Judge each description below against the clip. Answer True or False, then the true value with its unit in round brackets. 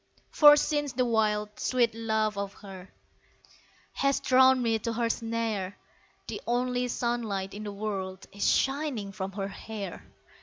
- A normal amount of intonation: True (3.6 semitones)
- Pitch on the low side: False (220 Hz)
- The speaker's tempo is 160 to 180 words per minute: False (145 wpm)